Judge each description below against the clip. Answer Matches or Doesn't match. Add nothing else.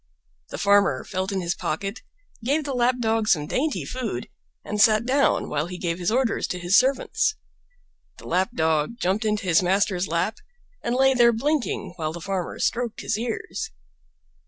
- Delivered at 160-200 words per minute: Matches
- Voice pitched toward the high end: Matches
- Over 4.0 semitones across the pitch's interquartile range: Matches